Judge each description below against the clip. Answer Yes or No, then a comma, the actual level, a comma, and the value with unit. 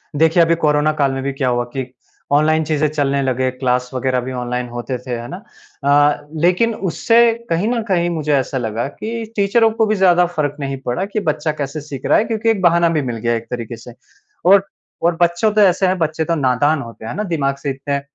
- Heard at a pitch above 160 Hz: No, medium, 150 Hz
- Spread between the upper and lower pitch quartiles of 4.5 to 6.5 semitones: Yes, average, 5.3 semitones